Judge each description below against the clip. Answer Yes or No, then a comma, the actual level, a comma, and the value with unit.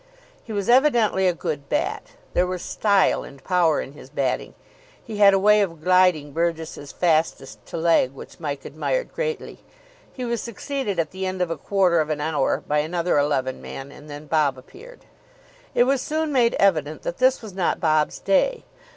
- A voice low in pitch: No, medium, 175 Hz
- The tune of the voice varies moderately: No, wide, 5.8 semitones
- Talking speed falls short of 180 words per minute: No, average, 185 wpm